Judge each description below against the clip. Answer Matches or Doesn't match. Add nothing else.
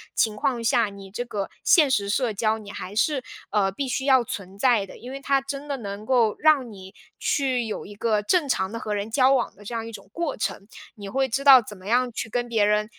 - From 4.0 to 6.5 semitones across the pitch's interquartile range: Matches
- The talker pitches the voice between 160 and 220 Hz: Doesn't match